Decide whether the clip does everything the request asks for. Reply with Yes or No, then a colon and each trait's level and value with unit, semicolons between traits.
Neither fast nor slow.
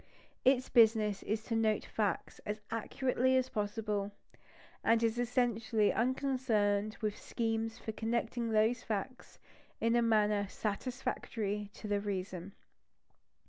No: slow, 125 wpm